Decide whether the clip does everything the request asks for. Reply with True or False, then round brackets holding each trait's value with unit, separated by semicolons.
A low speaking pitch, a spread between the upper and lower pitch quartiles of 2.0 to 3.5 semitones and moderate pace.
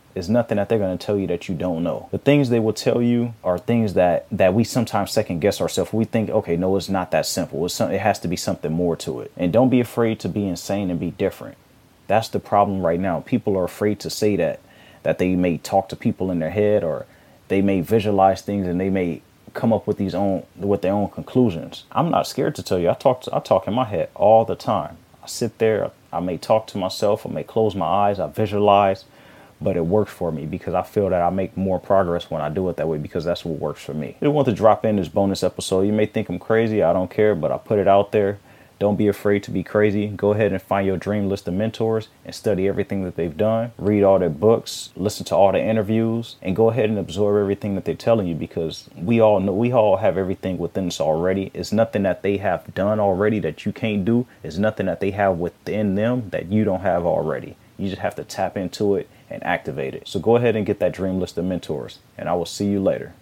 False (100 Hz; 2.6 semitones; 260 wpm)